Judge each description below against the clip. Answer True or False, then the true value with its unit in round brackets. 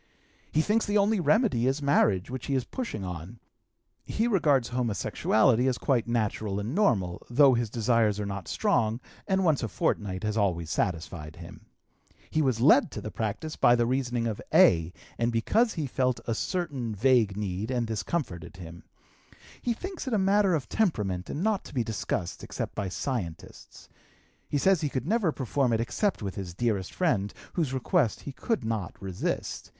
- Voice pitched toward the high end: False (120 Hz)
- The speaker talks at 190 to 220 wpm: False (180 wpm)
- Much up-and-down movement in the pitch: True (6.9 semitones)